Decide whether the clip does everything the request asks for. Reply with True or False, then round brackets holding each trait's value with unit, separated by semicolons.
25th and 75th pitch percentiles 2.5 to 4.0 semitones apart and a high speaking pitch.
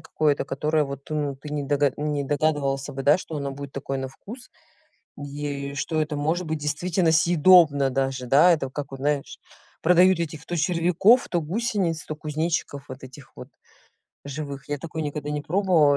False (2.8 semitones; 150 Hz)